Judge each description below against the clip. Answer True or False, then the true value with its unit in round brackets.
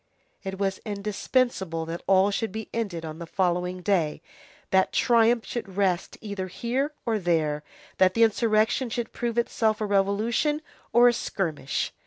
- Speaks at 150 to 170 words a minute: True (155 wpm)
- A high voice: True (200 Hz)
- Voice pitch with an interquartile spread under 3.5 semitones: False (4.0 semitones)